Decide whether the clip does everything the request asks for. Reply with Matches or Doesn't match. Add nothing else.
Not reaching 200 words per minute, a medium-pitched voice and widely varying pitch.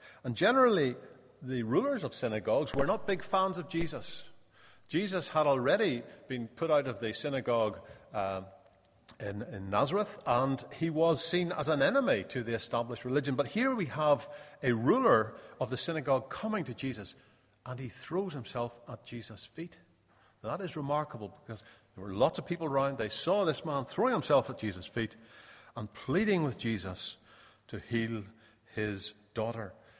Doesn't match